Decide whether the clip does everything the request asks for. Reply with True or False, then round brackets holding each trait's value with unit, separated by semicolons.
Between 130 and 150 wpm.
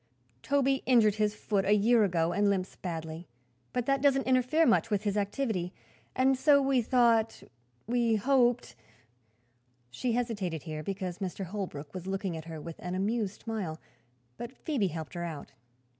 False (165 wpm)